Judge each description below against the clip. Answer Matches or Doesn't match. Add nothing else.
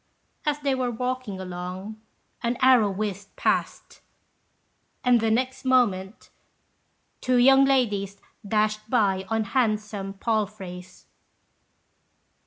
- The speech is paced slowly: Matches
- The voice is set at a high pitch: Matches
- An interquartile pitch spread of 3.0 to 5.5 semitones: Matches